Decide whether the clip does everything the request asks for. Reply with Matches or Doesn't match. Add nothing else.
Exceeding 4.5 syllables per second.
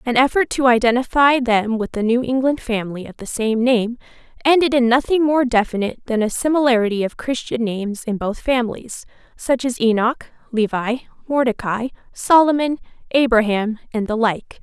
Matches